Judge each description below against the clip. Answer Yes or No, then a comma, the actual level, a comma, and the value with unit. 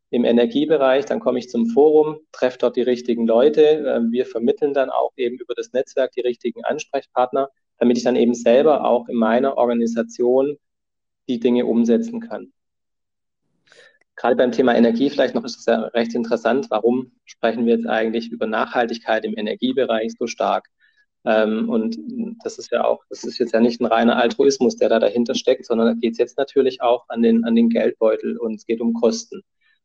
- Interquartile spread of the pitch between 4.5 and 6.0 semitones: Yes, average, 4.8 semitones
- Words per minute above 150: Yes, average, 185 wpm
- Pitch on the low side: Yes, low, 120 Hz